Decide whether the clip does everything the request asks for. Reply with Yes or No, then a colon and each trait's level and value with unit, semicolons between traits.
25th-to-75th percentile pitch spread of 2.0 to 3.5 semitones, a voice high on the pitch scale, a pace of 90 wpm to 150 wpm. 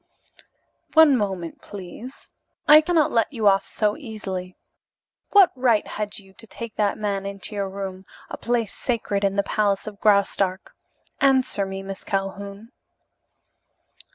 Yes: average, 3.1 semitones; high, 205 Hz; average, 140 wpm